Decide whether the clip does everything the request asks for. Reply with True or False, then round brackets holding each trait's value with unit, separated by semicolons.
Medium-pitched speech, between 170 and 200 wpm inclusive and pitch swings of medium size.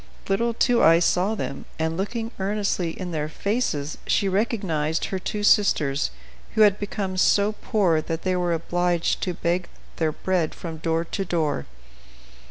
False (180 Hz; 160 wpm; 3.9 semitones)